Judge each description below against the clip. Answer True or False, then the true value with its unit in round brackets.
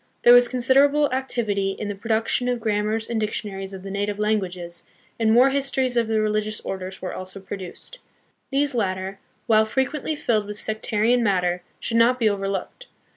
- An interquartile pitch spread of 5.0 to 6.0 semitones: False (3.8 semitones)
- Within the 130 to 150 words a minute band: False (170 wpm)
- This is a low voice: False (215 Hz)